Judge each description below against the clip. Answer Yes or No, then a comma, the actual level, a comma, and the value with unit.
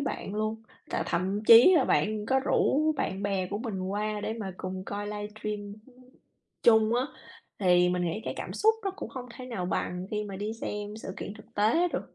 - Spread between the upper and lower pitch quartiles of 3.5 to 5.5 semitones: No, average, 2.7 semitones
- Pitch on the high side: Yes, high, 210 Hz